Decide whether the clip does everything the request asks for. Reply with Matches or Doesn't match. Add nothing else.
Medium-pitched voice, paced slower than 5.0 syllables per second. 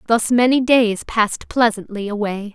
Doesn't match